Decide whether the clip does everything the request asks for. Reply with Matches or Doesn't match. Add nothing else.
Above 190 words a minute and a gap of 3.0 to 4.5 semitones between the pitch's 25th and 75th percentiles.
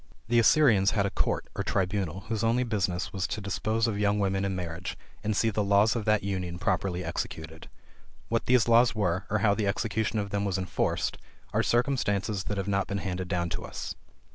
Doesn't match